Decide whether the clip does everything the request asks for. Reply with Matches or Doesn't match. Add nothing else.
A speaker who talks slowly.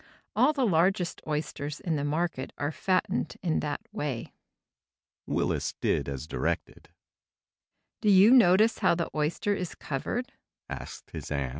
Matches